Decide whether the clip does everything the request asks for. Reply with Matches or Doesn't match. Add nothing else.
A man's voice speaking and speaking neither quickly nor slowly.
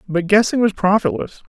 Matches